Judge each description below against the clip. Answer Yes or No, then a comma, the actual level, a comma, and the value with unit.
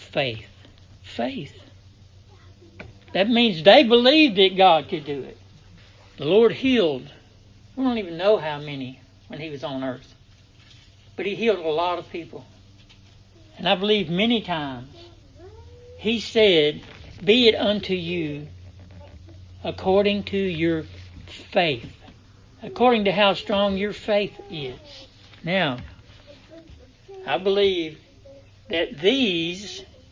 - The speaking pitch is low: Yes, low, 130 Hz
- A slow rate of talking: Yes, slow, 120 wpm